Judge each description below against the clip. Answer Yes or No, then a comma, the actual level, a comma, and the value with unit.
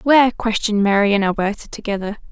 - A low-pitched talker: No, high, 215 Hz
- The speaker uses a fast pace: No, average, 155 wpm